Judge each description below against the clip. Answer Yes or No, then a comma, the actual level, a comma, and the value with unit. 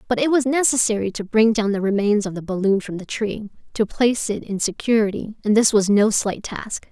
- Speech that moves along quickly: Yes, fast, 225 wpm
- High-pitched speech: Yes, high, 215 Hz